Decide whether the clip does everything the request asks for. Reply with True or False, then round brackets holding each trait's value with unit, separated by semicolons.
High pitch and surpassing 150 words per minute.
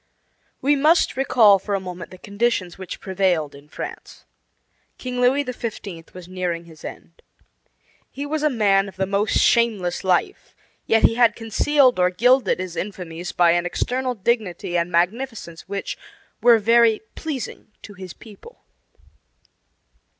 False (200 Hz; 145 wpm)